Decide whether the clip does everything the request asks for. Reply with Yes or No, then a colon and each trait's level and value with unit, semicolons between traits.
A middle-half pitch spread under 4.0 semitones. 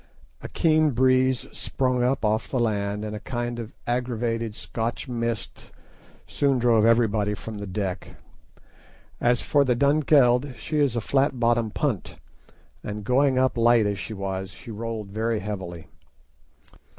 Yes: average, 3.3 semitones